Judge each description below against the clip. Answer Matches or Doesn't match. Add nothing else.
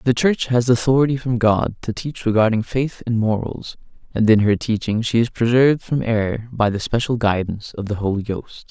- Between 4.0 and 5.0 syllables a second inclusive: Doesn't match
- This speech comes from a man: Matches